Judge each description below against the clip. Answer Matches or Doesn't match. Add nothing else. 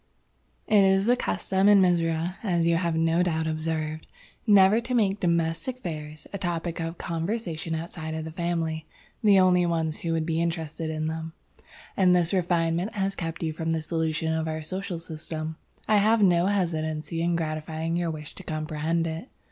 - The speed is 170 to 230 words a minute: Matches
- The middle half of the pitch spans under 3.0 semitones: Matches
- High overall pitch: Doesn't match